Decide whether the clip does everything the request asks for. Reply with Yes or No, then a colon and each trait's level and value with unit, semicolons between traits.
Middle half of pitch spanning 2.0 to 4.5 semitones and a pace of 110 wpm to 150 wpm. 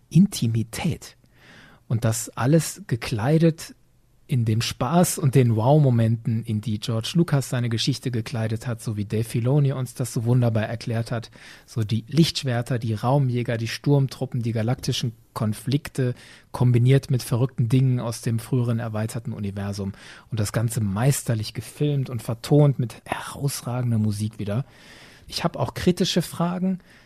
Yes: average, 3.2 semitones; average, 140 wpm